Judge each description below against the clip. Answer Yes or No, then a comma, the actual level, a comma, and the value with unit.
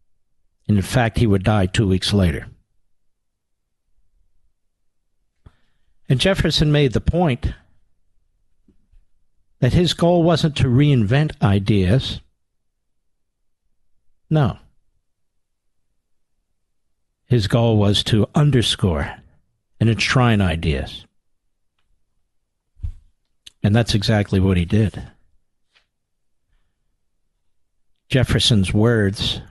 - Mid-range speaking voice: No, low, 100 Hz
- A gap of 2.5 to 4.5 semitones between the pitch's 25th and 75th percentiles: No, average, 5.1 semitones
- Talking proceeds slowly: Yes, slow, 75 wpm